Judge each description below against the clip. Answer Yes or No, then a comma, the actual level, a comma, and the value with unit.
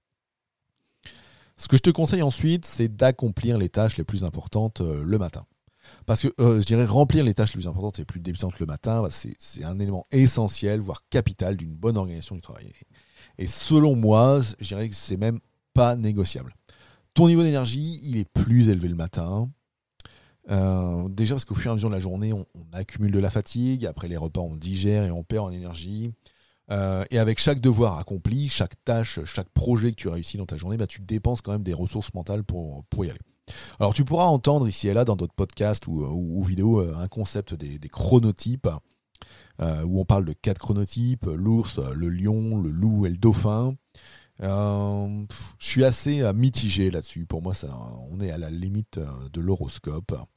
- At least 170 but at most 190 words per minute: No, average, 205 wpm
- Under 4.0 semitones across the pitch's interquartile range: No, average, 4.3 semitones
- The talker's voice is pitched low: Yes, low, 105 Hz